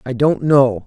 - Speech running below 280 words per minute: Yes, fast, 210 wpm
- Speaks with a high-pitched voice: No, low, 130 Hz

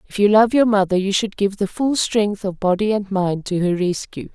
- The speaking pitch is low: No, high, 200 Hz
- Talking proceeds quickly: Yes, fast, 250 wpm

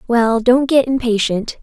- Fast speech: No, average, 150 wpm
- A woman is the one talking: Yes, female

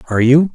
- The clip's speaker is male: Yes, male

